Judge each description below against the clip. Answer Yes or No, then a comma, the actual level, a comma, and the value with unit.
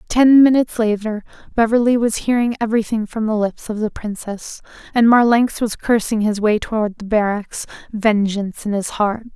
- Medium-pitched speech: No, high, 220 Hz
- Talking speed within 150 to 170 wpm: Yes, average, 165 wpm